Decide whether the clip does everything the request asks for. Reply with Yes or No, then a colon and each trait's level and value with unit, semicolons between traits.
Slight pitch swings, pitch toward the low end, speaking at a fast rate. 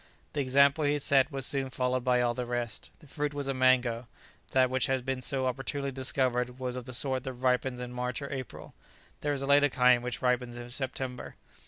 Yes: narrow, 1.6 semitones; low, 130 Hz; fast, 215 wpm